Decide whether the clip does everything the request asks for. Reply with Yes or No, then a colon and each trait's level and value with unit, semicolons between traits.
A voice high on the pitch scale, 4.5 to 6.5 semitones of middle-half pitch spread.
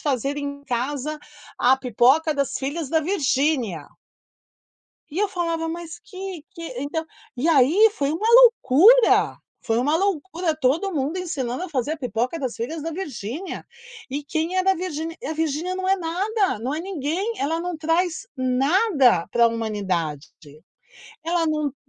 Yes: very high, 310 Hz; average, 4.9 semitones